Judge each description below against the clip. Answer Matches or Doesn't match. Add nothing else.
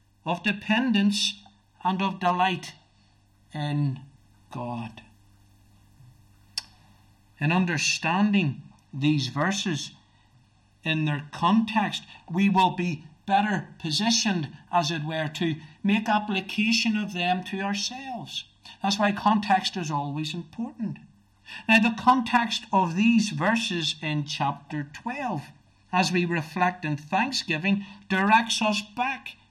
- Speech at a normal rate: Doesn't match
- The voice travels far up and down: Matches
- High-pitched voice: Doesn't match